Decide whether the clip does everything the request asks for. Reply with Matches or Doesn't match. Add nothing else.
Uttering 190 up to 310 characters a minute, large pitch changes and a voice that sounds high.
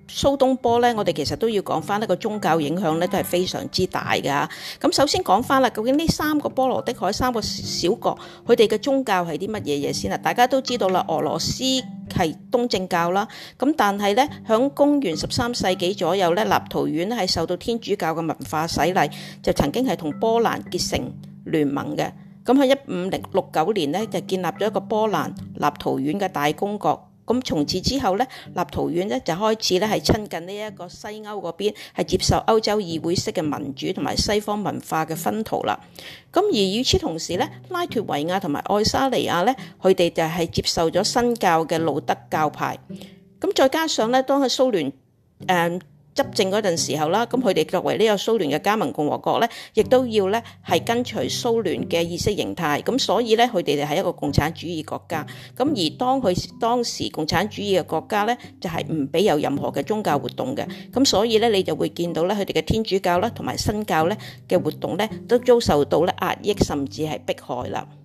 Matches